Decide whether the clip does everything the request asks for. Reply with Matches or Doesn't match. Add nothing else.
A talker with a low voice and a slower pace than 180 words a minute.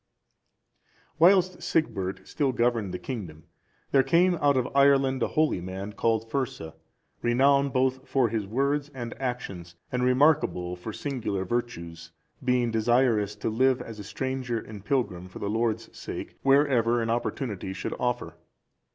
Matches